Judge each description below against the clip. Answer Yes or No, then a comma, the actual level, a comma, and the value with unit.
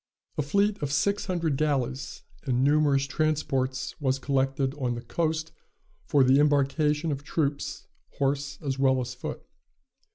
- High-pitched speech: No, medium, 140 Hz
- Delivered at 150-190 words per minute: No, average, 140 wpm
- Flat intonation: Yes, narrow, 2.3 semitones